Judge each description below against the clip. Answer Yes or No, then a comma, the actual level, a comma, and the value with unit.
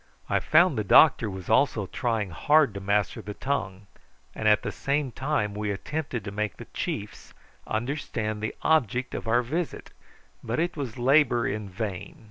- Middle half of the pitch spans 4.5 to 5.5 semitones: Yes, average, 5.2 semitones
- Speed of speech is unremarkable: Yes, average, 170 wpm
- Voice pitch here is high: No, low, 115 Hz